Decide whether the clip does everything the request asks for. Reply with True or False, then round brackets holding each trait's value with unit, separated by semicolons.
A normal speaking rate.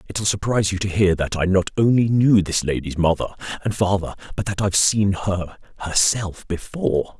True (185 wpm)